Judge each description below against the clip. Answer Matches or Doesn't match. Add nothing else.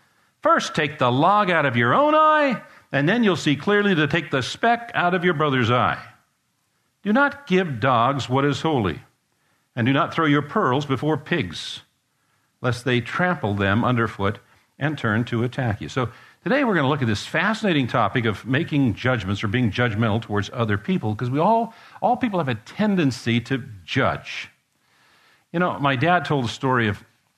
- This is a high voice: Doesn't match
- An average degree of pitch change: Doesn't match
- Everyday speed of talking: Matches